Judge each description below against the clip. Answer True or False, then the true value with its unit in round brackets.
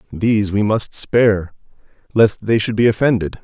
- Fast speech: False (155 wpm)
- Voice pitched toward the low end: True (105 Hz)